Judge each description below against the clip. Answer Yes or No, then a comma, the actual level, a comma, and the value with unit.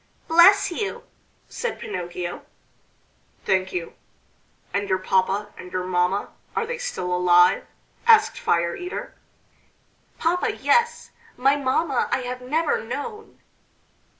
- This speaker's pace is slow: Yes, slow, 115 wpm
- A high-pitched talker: Yes, very high, 255 Hz